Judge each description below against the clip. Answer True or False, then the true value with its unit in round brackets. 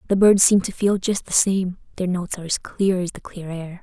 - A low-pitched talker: False (185 Hz)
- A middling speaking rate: False (265 wpm)